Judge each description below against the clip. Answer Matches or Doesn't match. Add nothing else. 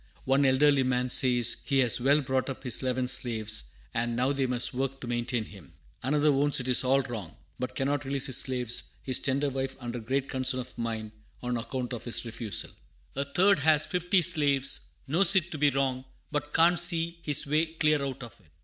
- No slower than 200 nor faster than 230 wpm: Matches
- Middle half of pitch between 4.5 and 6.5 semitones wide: Doesn't match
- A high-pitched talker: Doesn't match